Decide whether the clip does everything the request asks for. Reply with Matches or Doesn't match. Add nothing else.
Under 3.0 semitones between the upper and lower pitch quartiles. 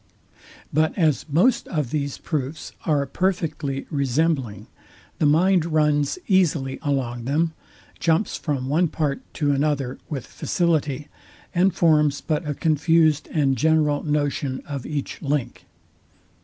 Matches